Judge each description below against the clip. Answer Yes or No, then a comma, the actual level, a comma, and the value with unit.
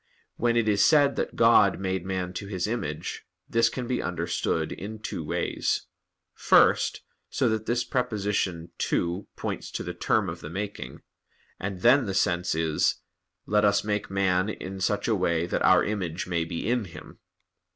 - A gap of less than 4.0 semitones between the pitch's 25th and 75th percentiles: Yes, average, 3.6 semitones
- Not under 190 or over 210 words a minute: No, average, 170 wpm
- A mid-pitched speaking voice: No, low, 100 Hz